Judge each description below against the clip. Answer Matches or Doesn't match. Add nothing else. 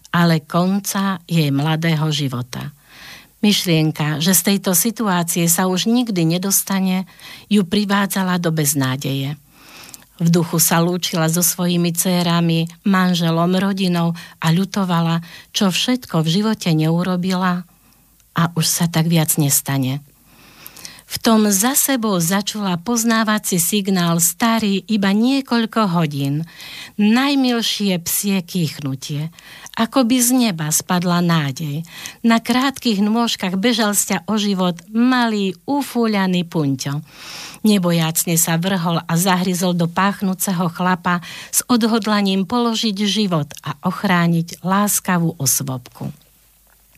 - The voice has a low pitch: Doesn't match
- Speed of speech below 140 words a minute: Matches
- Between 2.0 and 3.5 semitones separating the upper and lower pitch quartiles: Doesn't match